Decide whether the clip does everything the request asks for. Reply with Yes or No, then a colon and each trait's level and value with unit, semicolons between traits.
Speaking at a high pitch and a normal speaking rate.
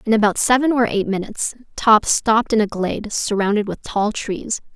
Yes: high, 215 Hz; average, 190 wpm